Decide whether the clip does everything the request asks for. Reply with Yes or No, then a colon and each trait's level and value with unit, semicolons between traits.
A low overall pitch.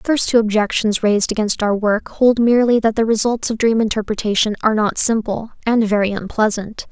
No: high, 220 Hz